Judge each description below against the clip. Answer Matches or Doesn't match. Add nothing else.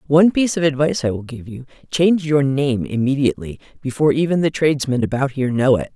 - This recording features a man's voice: Doesn't match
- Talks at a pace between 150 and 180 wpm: Doesn't match